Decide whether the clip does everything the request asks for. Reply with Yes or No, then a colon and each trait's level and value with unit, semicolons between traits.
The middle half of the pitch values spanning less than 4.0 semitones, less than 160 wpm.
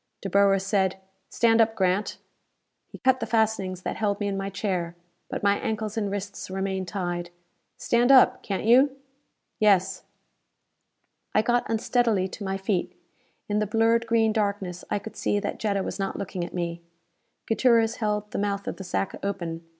No: narrow, 2.6 semitones; average, 175 wpm